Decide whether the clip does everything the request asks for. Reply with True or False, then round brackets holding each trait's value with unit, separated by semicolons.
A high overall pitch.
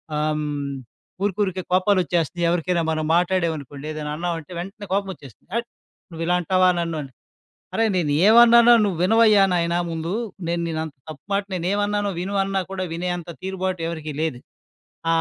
False (175 Hz)